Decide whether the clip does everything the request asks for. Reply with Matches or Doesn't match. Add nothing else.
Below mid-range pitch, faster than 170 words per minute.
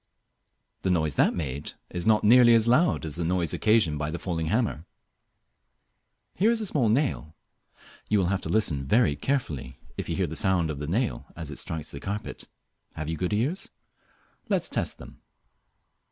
Matches